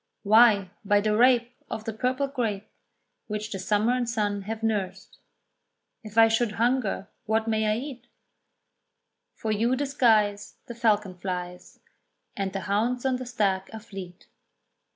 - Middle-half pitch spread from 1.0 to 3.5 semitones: Yes, average, 2.9 semitones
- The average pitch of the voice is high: Yes, high, 220 Hz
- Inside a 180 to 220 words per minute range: No, average, 150 wpm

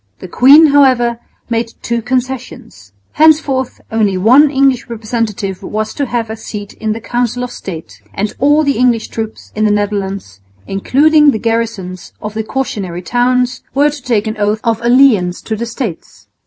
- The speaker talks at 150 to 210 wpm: Yes, average, 170 wpm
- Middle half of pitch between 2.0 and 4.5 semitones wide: Yes, average, 3.7 semitones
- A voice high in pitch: Yes, high, 230 Hz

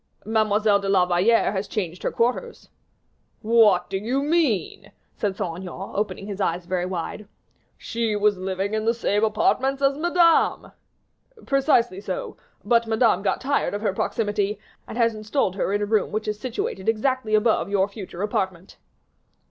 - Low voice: No, high, 210 Hz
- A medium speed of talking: Yes, average, 165 wpm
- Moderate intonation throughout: Yes, average, 3.2 semitones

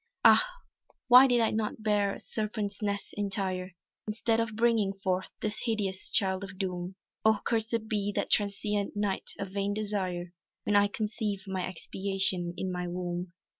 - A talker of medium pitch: No, high, 200 Hz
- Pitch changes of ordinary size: No, narrow, 2.2 semitones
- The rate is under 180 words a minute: Yes, average, 160 wpm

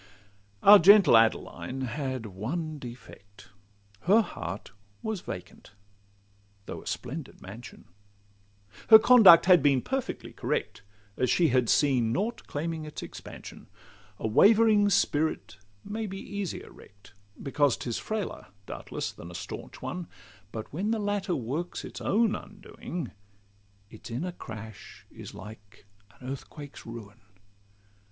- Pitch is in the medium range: Yes, medium, 145 Hz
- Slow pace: Yes, slow, 125 wpm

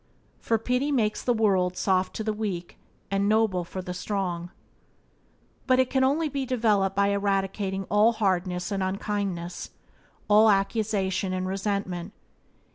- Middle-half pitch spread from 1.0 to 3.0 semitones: Yes, average, 2.7 semitones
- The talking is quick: No, average, 140 wpm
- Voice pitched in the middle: No, high, 200 Hz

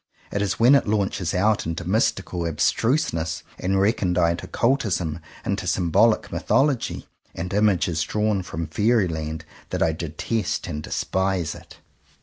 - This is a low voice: Yes, very low, 95 Hz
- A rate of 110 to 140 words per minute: Yes, slow, 135 wpm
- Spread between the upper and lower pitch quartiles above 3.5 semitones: Yes, average, 4.5 semitones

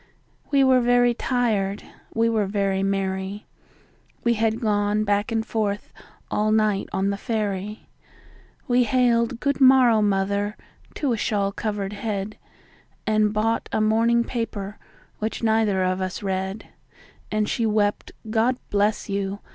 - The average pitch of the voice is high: Yes, high, 215 Hz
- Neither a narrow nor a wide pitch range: No, narrow, 2.3 semitones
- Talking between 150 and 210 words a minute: No, average, 140 wpm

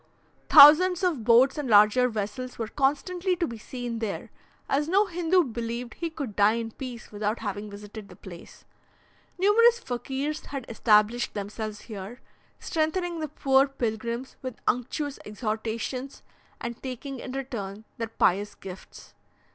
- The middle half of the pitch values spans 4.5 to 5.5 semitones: Yes, average, 5.2 semitones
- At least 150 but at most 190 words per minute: No, average, 140 wpm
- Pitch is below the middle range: No, high, 245 Hz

